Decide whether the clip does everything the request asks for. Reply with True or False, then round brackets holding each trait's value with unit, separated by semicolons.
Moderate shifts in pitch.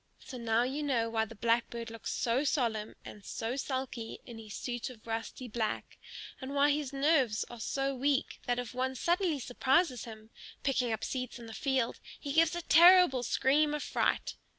True (3.5 semitones)